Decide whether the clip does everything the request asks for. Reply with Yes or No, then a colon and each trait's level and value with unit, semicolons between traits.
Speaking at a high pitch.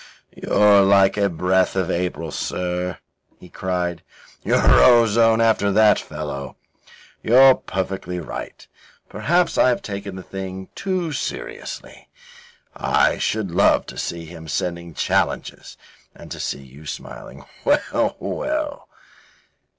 No: very low, 95 Hz